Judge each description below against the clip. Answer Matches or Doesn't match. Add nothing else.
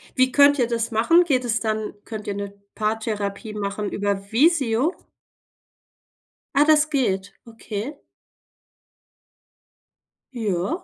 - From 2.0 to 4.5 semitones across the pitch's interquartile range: Doesn't match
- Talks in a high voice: Matches